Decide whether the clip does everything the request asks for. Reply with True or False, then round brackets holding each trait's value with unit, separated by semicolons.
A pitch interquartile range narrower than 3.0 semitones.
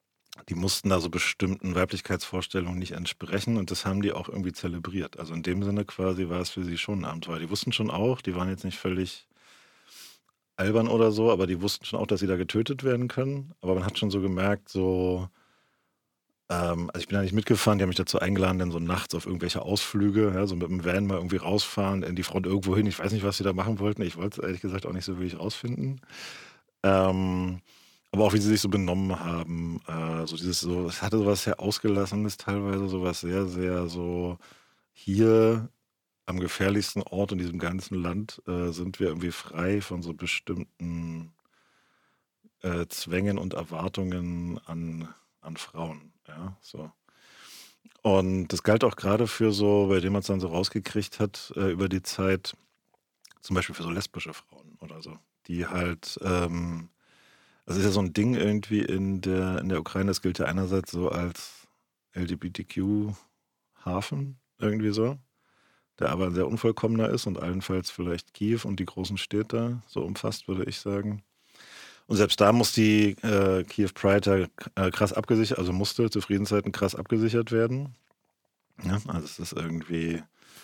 True (2.6 semitones)